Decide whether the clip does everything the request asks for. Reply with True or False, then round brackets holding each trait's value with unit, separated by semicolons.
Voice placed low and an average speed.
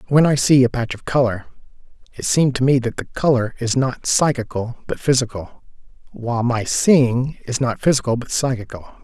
True (125 Hz; 180 wpm)